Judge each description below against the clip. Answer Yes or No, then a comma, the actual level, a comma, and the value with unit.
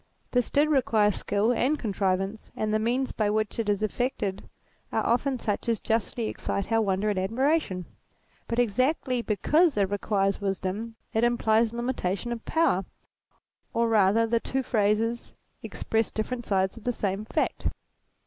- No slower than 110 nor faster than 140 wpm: No, average, 155 wpm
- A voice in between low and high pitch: No, high, 225 Hz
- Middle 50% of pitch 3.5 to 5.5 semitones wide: No, average, 3.0 semitones